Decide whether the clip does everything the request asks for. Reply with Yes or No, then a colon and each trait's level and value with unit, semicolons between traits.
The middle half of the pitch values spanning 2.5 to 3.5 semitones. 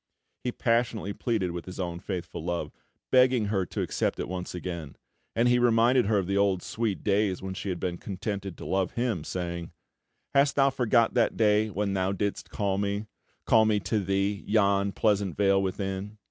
Yes: average, 2.9 semitones